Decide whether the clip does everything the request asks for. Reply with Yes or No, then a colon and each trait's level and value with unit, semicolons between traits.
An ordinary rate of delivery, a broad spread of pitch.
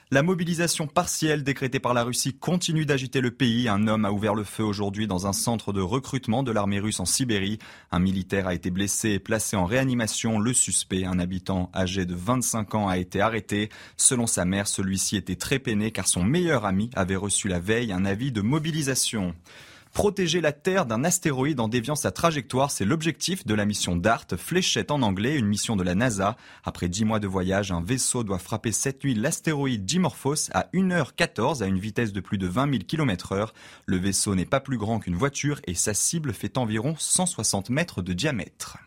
Yes: average, 205 wpm; wide, 5.8 semitones